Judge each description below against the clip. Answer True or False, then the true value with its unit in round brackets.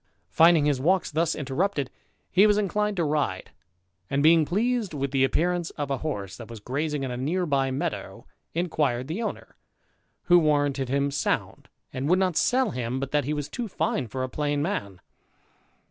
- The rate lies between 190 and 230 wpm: False (180 wpm)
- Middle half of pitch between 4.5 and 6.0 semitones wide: True (4.8 semitones)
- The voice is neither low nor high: True (150 Hz)